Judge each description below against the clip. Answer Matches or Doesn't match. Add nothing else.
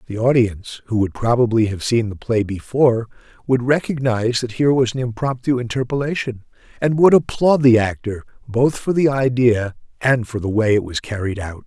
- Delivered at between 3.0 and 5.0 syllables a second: Doesn't match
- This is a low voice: Matches